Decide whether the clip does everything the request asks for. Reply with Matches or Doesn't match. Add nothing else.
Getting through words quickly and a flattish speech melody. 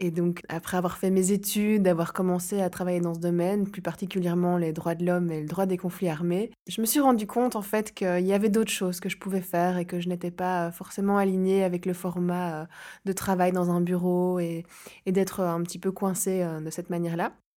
Matches